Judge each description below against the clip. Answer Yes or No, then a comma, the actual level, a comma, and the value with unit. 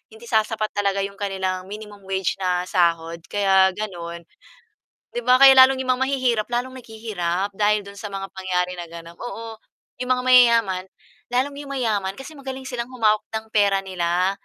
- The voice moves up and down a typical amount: Yes, average, 4.2 semitones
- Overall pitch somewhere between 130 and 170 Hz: No, high, 205 Hz